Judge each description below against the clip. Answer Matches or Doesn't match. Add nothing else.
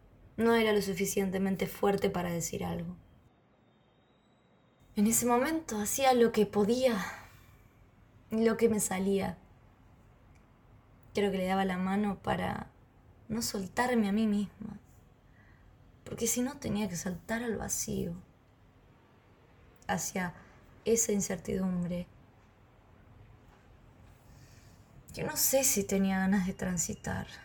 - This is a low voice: Doesn't match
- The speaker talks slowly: Matches